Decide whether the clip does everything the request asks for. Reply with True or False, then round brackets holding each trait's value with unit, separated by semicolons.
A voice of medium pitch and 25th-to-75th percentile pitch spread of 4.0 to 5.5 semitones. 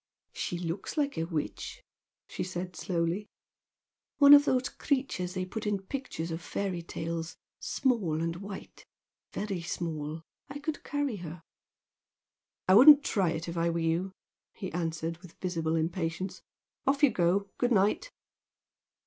True (180 Hz; 4.8 semitones)